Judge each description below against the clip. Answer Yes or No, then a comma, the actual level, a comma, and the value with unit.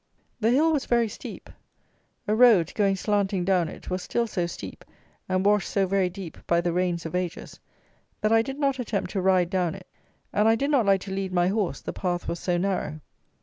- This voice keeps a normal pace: No, fast, 215 wpm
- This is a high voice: Yes, high, 195 Hz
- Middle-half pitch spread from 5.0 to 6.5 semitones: No, average, 3.4 semitones